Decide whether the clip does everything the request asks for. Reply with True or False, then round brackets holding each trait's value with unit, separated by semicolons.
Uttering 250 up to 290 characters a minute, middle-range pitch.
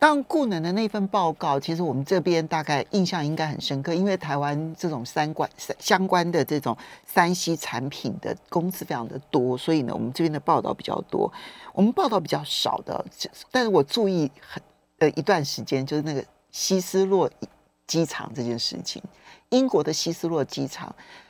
True (280 characters per minute; 160 Hz)